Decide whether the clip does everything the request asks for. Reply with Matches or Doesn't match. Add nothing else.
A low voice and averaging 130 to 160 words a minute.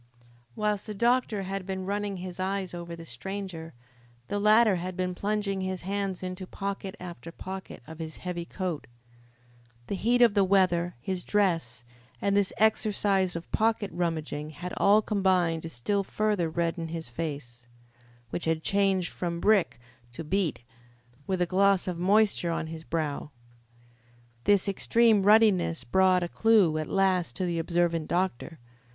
Doesn't match